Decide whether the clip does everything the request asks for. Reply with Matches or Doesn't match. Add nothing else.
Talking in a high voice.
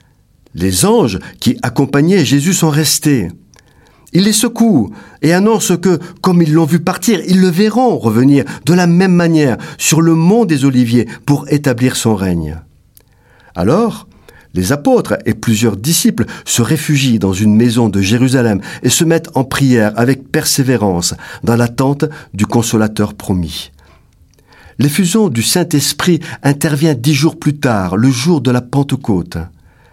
Doesn't match